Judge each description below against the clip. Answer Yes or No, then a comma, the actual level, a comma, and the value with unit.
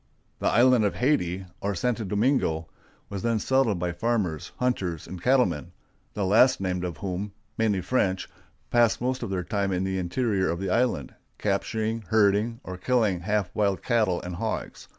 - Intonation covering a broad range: No, average, 4.3 semitones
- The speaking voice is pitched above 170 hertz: No, low, 100 Hz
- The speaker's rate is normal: Yes, average, 170 wpm